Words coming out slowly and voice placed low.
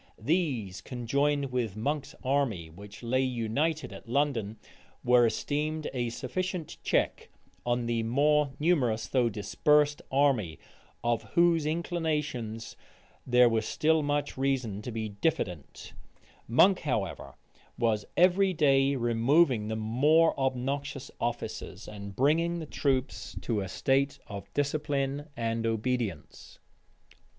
Yes: slow, 120 wpm; low, 130 Hz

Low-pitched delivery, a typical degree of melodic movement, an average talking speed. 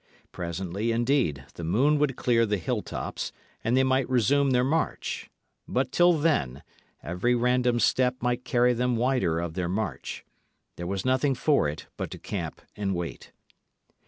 No: low, 120 Hz; wide, 6.0 semitones; average, 160 wpm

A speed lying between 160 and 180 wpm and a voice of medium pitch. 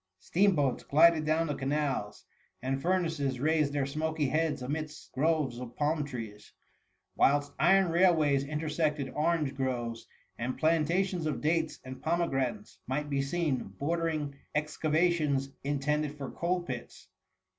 No: slow, 135 wpm; medium, 150 Hz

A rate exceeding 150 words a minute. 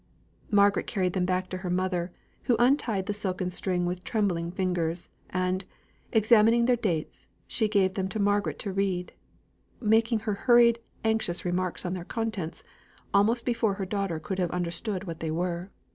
Yes: average, 165 wpm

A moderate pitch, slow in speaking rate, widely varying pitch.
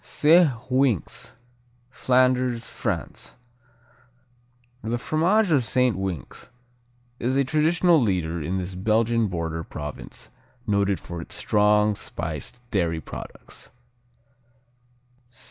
No: low, 110 Hz; slow, 95 wpm; wide, 6.1 semitones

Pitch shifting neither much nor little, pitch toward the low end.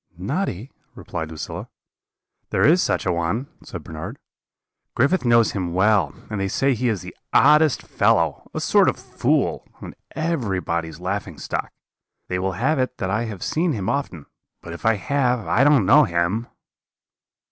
No: wide, 6.4 semitones; low, 105 Hz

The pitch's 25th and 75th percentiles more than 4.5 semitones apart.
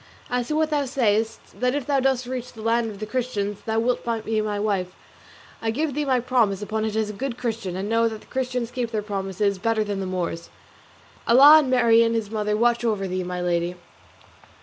No: average, 3.4 semitones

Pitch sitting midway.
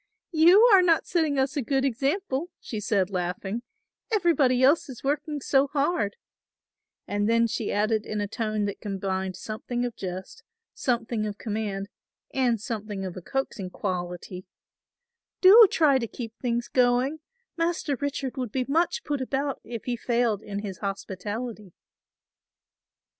No: high, 240 Hz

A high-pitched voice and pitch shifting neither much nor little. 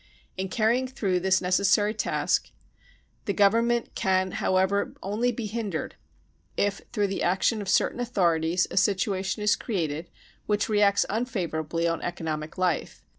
Yes: high, 195 Hz; average, 3.0 semitones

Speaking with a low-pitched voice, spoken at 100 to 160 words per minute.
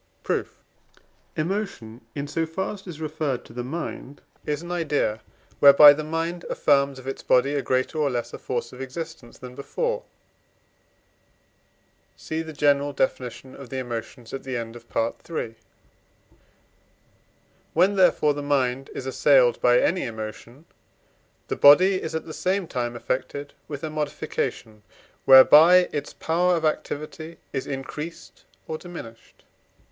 No: medium, 145 Hz; average, 145 wpm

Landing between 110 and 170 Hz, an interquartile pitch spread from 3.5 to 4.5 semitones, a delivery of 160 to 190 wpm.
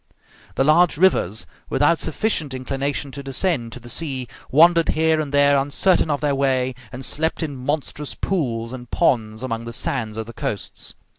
Yes: medium, 140 Hz; average, 3.9 semitones; average, 170 wpm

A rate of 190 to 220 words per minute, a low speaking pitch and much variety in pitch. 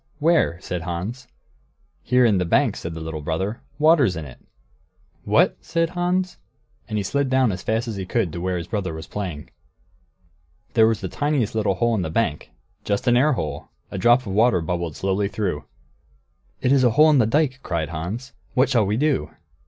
Yes: average, 200 wpm; low, 105 Hz; wide, 6.6 semitones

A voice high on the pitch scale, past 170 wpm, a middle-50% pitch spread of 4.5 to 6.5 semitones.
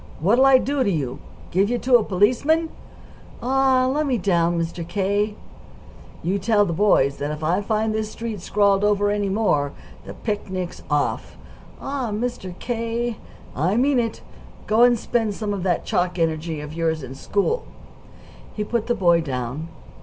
No: high, 205 Hz; average, 165 wpm; wide, 5.5 semitones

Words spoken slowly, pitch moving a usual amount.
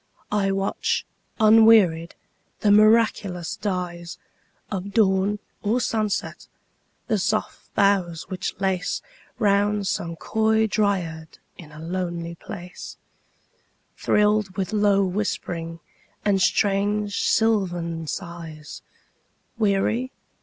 Yes: slow, 80 wpm; average, 3.4 semitones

